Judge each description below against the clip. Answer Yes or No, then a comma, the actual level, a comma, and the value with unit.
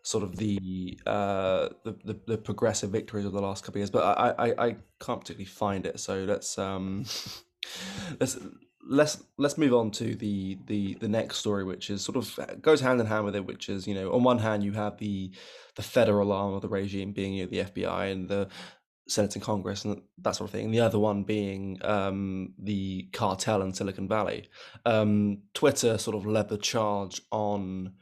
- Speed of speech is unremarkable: No, fast, 210 wpm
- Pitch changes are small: Yes, narrow, 1.9 semitones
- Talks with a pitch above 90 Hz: Yes, low, 100 Hz